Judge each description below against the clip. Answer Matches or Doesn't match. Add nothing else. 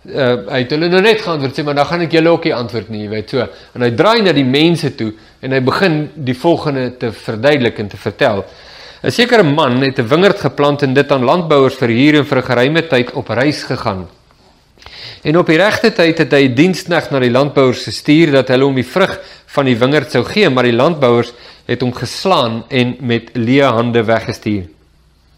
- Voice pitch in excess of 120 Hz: Matches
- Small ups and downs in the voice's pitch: Doesn't match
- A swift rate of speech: Matches